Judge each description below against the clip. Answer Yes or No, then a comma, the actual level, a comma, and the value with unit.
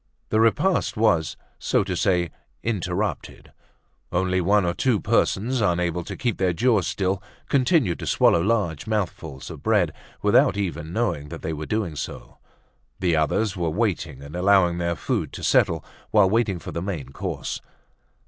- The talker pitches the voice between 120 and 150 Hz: No, very low, 95 Hz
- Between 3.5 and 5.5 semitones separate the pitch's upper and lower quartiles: Yes, average, 4.1 semitones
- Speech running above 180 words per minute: No, average, 160 wpm